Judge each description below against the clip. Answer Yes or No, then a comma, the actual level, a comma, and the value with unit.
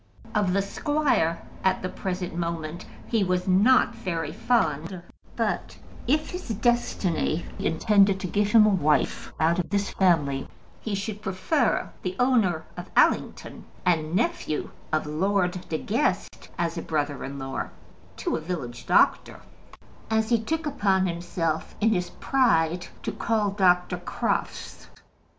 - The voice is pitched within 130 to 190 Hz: Yes, medium, 185 Hz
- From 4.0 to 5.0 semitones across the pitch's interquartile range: Yes, average, 4.4 semitones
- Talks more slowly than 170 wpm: Yes, average, 140 wpm